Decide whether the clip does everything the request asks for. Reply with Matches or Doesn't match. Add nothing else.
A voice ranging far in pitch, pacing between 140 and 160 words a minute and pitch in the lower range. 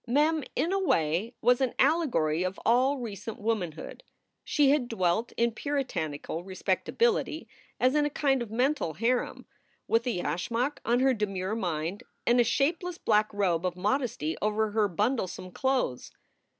Doesn't match